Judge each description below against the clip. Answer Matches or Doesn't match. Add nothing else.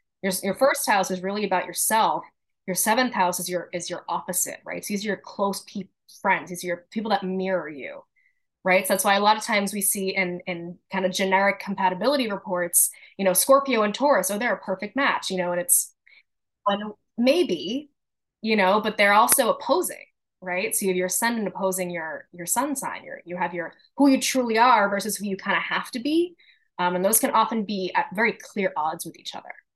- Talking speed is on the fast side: Matches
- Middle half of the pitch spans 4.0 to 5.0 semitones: Doesn't match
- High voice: Matches